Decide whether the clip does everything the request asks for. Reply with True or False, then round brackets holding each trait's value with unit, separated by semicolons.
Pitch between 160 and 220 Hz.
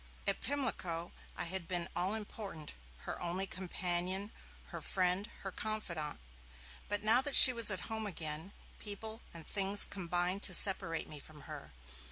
True (190 Hz)